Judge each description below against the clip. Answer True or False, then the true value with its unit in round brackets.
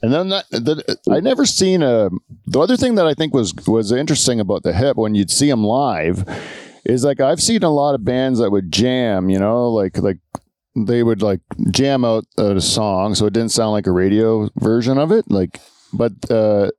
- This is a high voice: False (115 Hz)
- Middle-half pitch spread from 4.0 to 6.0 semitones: True (5.0 semitones)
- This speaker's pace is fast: True (210 wpm)